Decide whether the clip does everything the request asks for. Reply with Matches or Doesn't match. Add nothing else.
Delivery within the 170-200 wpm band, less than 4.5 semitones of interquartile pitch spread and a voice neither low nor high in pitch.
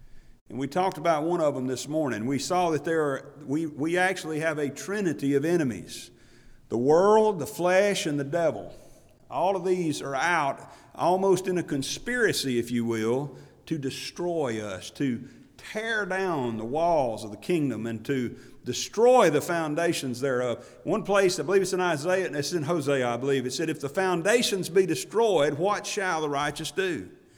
Doesn't match